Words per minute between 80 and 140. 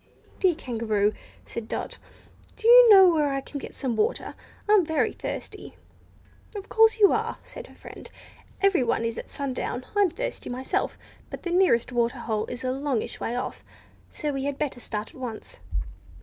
No: average, 175 wpm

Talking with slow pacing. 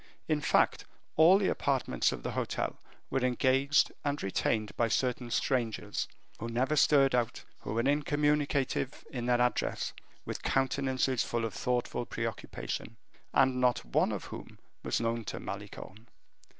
No: average, 145 wpm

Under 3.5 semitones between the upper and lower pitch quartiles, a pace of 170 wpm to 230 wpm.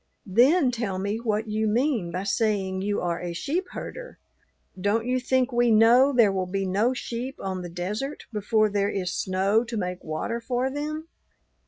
No: average, 4.5 semitones; average, 180 wpm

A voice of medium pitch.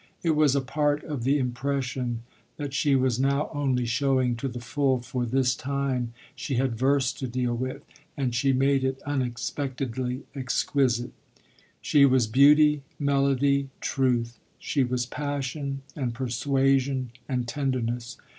No: low, 130 Hz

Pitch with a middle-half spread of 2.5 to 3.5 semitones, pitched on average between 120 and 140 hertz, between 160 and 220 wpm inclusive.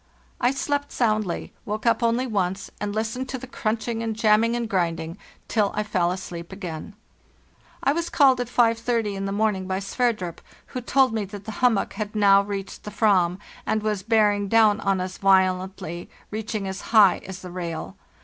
No: average, 3.1 semitones; high, 210 Hz; average, 180 wpm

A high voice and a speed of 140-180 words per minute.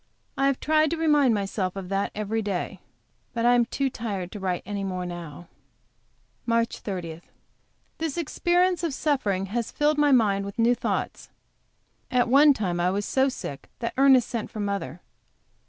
Yes: high, 225 Hz; average, 170 wpm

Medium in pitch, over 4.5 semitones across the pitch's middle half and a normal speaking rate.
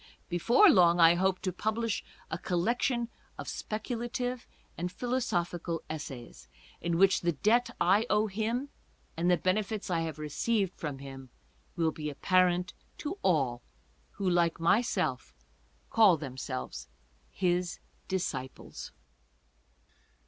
No: medium, 180 Hz; average, 4.9 semitones; slow, 120 wpm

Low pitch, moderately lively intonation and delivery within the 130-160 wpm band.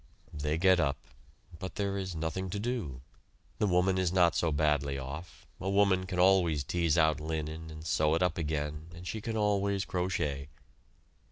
No: very low, 85 Hz; average, 3.7 semitones; average, 175 wpm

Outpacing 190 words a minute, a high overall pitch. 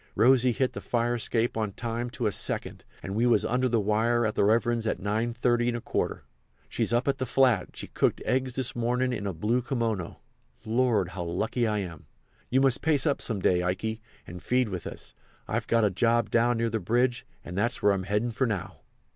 No: average, 200 wpm; low, 115 Hz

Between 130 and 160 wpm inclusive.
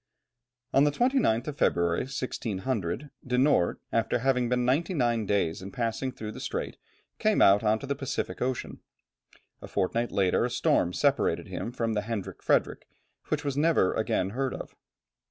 No: average, 170 wpm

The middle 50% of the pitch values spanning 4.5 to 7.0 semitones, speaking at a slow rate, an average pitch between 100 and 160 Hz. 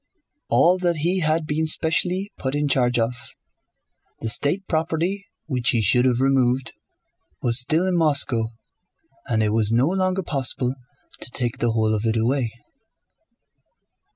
No: wide, 5.5 semitones; average, 150 wpm; low, 135 Hz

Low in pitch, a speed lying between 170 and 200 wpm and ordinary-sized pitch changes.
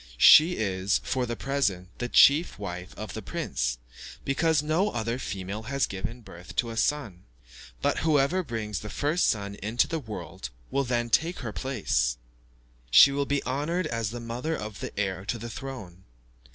No: low, 115 Hz; average, 175 wpm; wide, 5.7 semitones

